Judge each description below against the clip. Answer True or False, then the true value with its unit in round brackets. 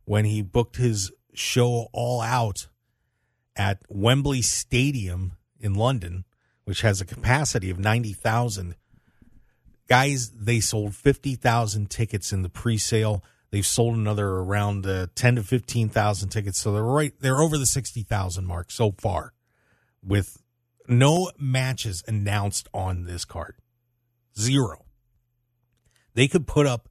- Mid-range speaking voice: False (115 Hz)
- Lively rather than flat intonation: False (3.3 semitones)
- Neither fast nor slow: False (130 wpm)